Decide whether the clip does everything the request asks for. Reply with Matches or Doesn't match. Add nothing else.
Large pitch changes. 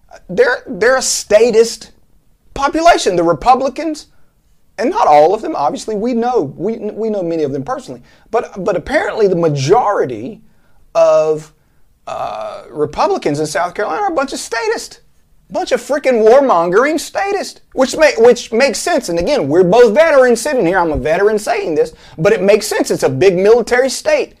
Matches